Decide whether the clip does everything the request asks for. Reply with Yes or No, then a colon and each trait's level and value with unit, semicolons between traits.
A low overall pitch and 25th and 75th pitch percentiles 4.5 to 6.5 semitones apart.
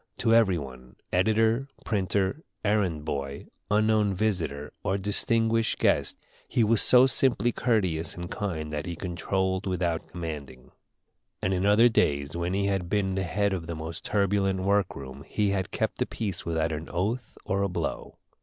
No: very low, 95 Hz; average, 4.1 semitones